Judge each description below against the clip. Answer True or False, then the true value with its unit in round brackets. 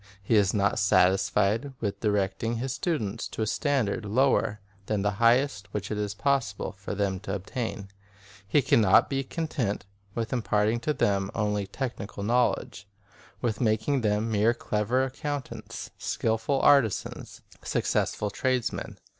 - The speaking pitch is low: True (110 Hz)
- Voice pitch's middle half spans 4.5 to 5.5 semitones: False (3.8 semitones)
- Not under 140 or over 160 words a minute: True (145 wpm)